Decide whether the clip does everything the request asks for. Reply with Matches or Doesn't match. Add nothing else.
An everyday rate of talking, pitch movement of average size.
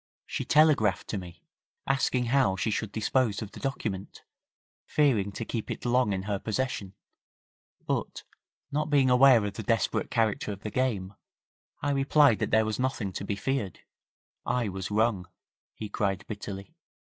Matches